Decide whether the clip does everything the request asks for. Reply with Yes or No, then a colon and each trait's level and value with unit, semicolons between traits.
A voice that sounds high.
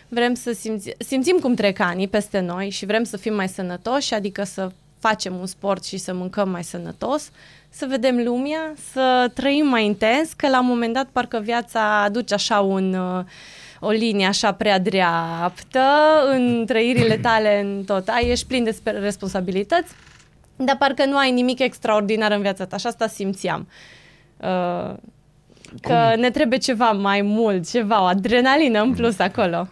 Yes: high, 220 Hz